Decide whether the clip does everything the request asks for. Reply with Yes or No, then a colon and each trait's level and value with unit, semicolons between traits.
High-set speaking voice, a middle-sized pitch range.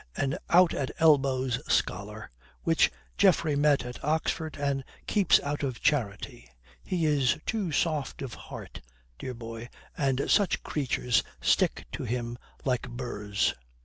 No: low, 135 Hz; average, 4.1 semitones